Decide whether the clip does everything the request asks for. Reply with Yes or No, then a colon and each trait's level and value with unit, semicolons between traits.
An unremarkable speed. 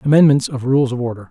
No: fast, 230 wpm